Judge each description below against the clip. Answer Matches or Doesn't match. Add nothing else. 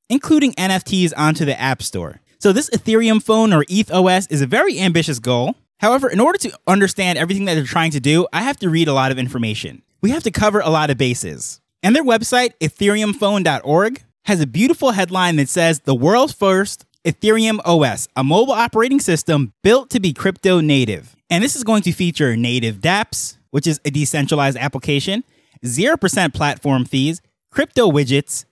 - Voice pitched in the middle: Matches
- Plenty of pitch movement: Matches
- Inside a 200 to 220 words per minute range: Doesn't match